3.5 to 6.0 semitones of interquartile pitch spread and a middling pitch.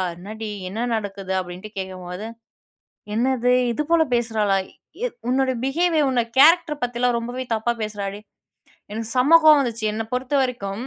No: average, 4.1 semitones; high, 235 Hz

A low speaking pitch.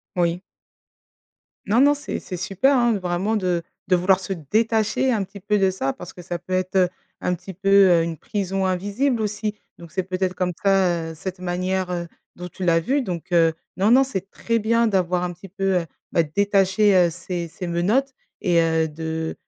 No: medium, 185 Hz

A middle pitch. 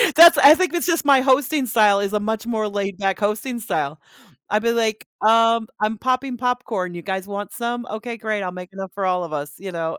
No: high, 215 Hz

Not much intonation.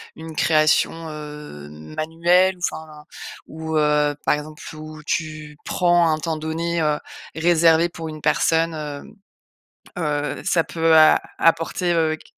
Yes: narrow, 1.5 semitones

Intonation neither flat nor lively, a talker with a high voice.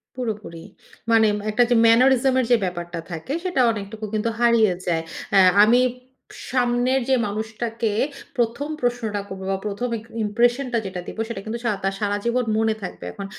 Yes: average, 3.0 semitones; high, 225 Hz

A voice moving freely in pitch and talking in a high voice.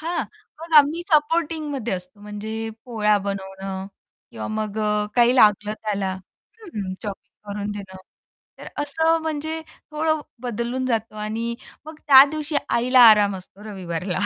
Yes: wide, 6.4 semitones; high, 220 Hz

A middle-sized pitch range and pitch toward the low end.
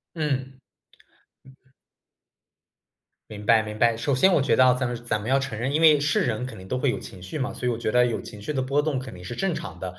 Yes: average, 4.2 semitones; low, 125 Hz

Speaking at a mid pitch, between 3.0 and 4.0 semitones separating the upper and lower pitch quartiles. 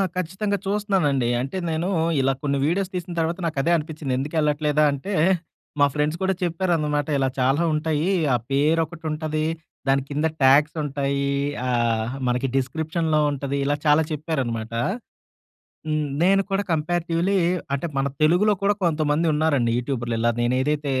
Yes: medium, 150 Hz; average, 3.4 semitones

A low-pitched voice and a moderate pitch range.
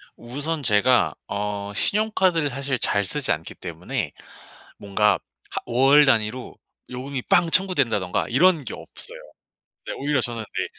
No: low, 130 Hz; wide, 5.9 semitones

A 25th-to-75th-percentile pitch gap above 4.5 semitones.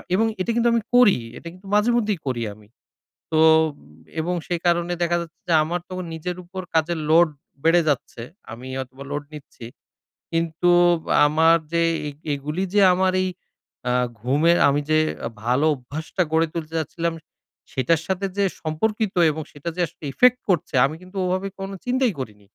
No: average, 3.8 semitones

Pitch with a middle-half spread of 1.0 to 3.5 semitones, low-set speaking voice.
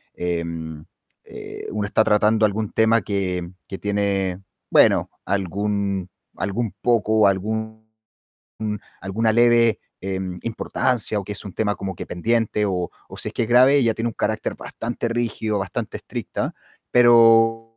Yes: average, 2.8 semitones; low, 105 Hz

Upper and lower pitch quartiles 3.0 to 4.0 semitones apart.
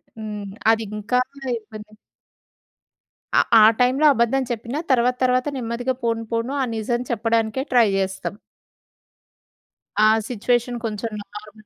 No: narrow, 2.5 semitones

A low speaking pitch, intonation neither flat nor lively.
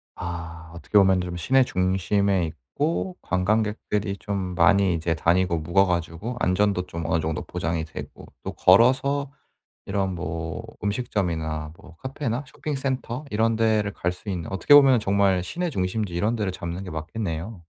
Yes: very low, 95 Hz; average, 4.5 semitones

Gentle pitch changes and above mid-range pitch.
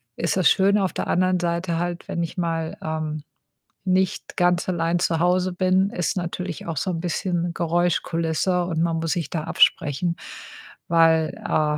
No: narrow, 1.8 semitones; medium, 170 Hz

